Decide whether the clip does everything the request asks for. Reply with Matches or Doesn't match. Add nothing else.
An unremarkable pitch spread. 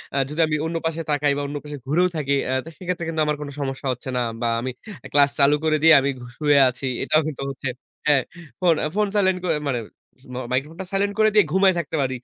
Matches